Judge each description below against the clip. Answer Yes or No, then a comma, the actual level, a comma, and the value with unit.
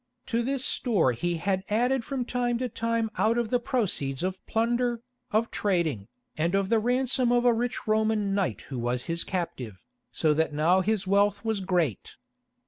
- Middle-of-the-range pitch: No, high, 210 Hz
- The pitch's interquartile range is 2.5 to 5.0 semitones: No, wide, 5.6 semitones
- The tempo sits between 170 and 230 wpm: Yes, average, 180 wpm